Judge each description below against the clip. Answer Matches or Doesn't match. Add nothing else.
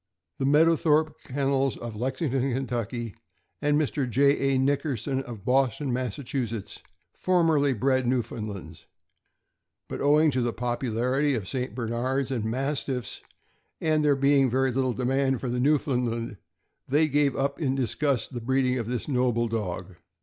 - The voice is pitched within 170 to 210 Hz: Doesn't match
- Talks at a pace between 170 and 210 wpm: Doesn't match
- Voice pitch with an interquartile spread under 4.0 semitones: Matches